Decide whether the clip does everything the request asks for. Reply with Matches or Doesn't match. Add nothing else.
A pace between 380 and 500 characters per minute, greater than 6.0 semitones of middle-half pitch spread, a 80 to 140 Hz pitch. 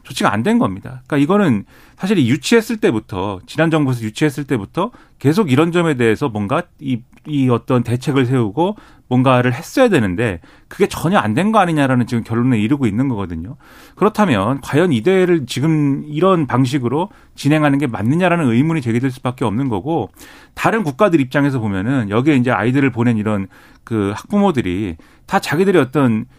Doesn't match